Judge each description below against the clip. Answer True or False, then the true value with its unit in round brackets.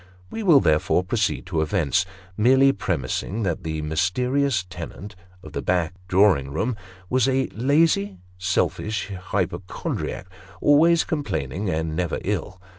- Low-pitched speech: True (95 Hz)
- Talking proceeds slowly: True (125 wpm)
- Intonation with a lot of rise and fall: True (6.6 semitones)